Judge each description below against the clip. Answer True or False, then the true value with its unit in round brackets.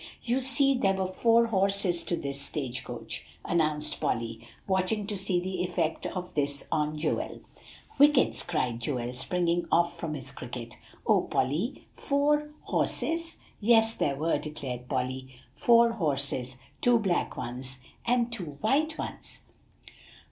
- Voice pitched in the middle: True (175 Hz)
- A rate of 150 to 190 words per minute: False (140 wpm)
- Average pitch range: False (8.5 semitones)